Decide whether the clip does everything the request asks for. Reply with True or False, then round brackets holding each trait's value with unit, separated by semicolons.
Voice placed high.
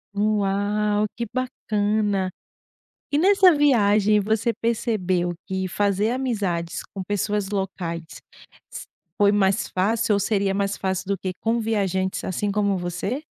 True (205 Hz)